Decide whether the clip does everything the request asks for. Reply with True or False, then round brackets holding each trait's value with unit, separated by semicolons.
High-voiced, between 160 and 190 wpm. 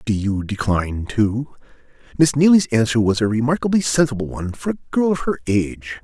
False (120 Hz; 180 wpm)